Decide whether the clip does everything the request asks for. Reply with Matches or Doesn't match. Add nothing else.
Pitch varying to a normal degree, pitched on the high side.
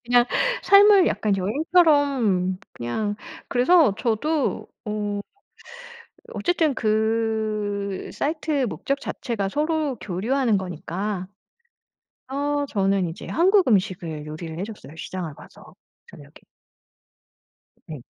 Doesn't match